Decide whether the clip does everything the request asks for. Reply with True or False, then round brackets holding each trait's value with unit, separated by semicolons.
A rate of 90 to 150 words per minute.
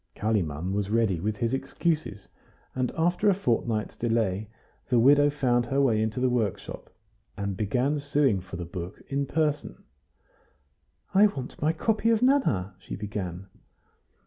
True (145 wpm)